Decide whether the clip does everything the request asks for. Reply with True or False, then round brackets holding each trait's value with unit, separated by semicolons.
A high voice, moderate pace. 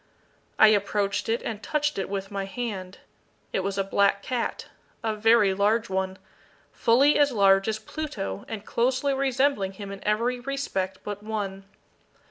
True (210 Hz; 155 wpm)